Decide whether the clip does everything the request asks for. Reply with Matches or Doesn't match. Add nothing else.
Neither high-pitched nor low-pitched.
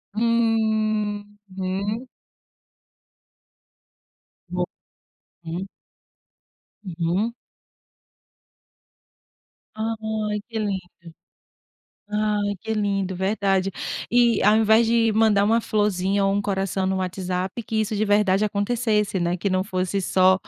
Doesn't match